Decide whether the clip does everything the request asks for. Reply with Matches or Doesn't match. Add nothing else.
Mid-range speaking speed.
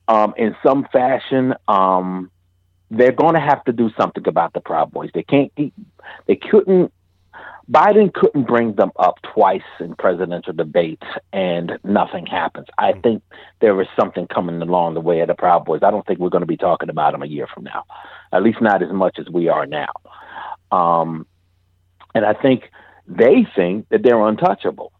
Matches